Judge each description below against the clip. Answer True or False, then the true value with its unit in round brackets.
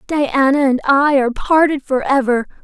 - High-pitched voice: True (275 Hz)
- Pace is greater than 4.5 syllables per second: True (4.8 syllables/s)